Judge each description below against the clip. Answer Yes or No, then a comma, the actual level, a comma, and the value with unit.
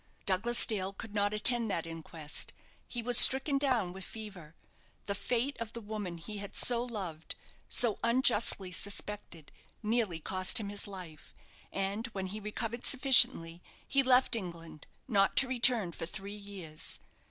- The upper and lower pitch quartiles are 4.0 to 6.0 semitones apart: Yes, average, 4.4 semitones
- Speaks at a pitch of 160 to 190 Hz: No, high, 205 Hz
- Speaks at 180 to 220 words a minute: No, average, 155 wpm